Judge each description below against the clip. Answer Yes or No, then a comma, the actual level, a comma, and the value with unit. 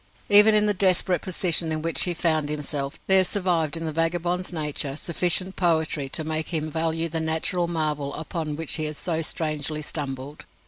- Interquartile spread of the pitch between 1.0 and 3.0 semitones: Yes, narrow, 2.4 semitones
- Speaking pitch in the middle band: Yes, medium, 160 Hz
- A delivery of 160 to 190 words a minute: Yes, average, 180 wpm